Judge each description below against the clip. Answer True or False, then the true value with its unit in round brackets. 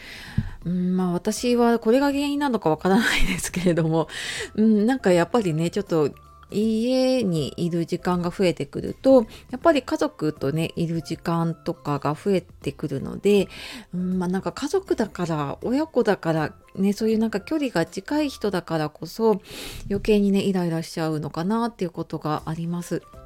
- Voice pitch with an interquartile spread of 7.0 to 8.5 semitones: False (5.3 semitones)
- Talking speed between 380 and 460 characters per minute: False (350 characters per minute)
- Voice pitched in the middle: True (180 Hz)